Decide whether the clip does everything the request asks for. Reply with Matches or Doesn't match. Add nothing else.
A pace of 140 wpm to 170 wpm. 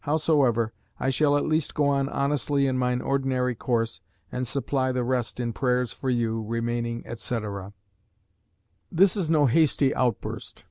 Matches